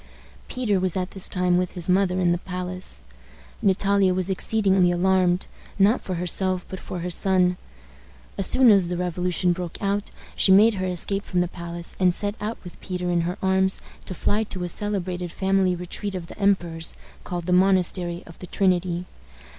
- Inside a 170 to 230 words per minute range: Yes, average, 185 wpm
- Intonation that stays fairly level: Yes, narrow, 1.6 semitones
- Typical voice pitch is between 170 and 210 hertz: Yes, medium, 185 Hz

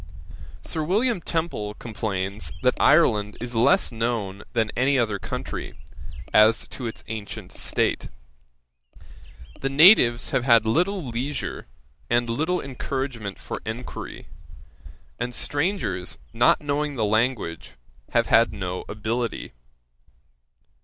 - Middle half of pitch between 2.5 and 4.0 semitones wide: No, average, 4.8 semitones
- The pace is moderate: No, slow, 110 wpm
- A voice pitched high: No, low, 120 Hz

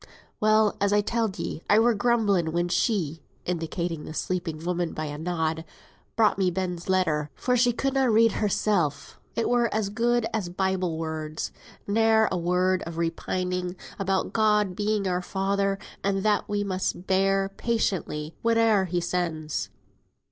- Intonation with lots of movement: No, average, 3.8 semitones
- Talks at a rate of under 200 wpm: Yes, average, 160 wpm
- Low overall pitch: No, high, 190 Hz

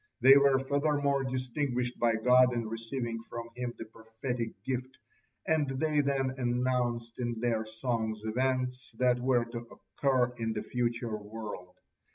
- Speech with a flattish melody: Yes, narrow, 2.3 semitones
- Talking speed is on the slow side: No, average, 145 wpm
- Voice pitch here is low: Yes, low, 125 Hz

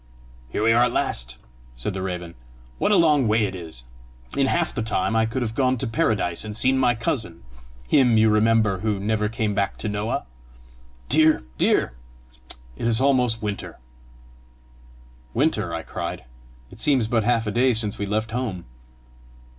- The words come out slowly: No, average, 170 wpm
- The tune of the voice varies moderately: Yes, average, 3.2 semitones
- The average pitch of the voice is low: Yes, low, 110 Hz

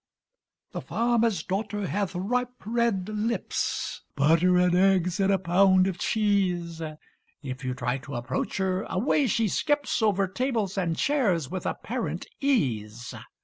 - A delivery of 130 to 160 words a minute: Yes, average, 140 wpm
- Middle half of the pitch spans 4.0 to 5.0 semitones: Yes, average, 4.3 semitones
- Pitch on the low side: No, high, 190 Hz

